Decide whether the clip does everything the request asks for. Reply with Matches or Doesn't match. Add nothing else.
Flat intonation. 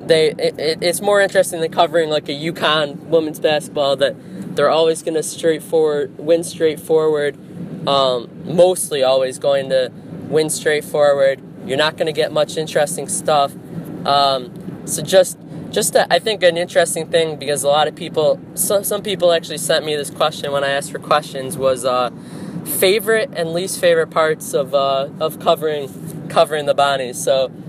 Doesn't match